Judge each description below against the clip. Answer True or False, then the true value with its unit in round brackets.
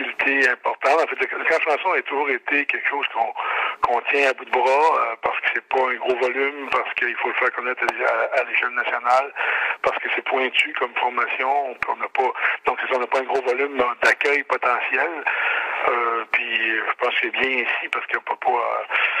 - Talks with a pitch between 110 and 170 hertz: True (140 Hz)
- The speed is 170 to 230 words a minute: True (210 wpm)